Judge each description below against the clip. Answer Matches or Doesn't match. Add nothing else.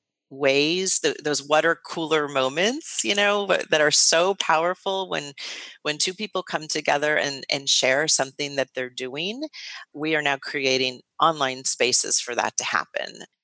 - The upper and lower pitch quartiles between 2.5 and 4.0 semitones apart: Doesn't match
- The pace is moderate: Matches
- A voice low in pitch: Doesn't match